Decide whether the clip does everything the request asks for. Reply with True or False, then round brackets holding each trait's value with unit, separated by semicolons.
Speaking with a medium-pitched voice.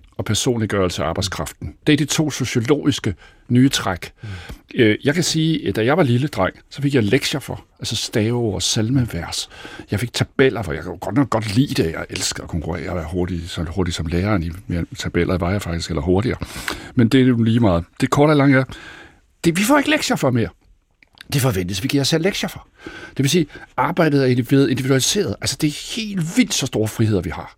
False (120 Hz)